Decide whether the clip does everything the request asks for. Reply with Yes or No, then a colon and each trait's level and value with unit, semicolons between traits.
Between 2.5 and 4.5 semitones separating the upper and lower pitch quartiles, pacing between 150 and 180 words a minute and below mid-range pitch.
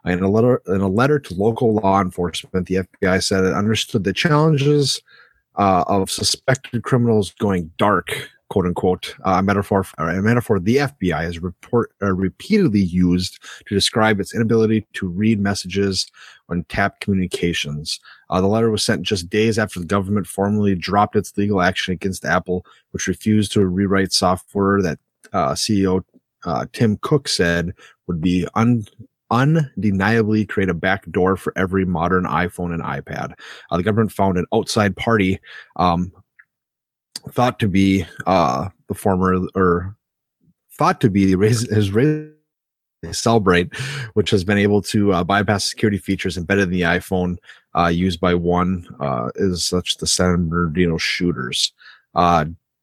Yes: average, 3.1 semitones; average, 155 wpm; very low, 95 Hz